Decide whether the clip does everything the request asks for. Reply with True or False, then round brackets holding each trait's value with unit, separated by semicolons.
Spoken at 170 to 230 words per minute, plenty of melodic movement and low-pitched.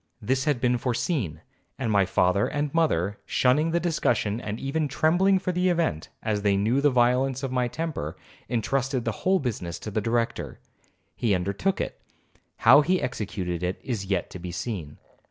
True (175 wpm; 6.5 semitones; 120 Hz)